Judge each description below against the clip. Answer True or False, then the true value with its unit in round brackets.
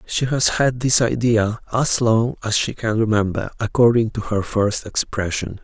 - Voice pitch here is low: True (110 Hz)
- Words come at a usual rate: True (170 wpm)